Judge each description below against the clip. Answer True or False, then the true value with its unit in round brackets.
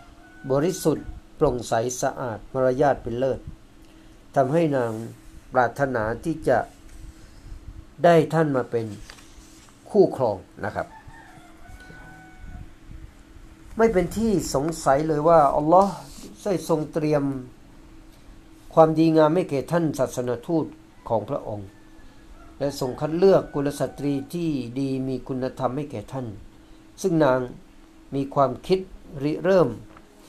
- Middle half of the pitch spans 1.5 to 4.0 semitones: False (4.4 semitones)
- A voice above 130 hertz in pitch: True (140 Hz)